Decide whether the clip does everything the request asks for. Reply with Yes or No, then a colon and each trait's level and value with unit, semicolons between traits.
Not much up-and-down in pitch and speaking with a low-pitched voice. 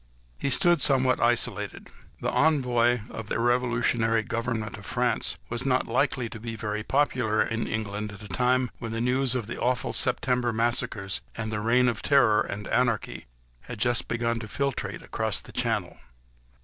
Yes: narrow, 2.3 semitones; low, 120 Hz